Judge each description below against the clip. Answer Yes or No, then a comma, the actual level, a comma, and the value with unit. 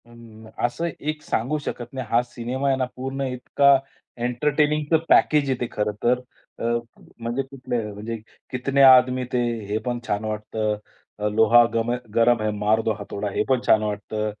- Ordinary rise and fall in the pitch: Yes, average, 3.3 semitones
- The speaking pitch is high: No, low, 120 Hz